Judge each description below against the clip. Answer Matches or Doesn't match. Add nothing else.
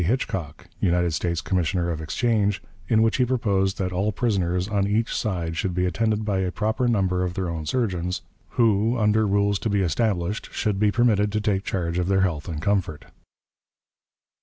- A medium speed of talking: Matches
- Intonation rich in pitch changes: Doesn't match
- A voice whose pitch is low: Matches